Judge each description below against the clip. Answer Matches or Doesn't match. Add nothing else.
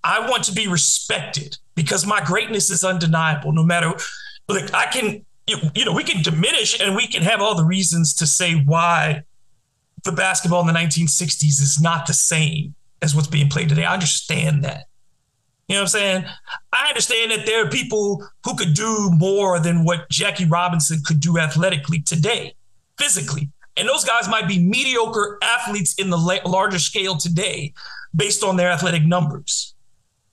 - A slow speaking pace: Doesn't match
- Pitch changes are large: Doesn't match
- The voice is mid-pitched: Matches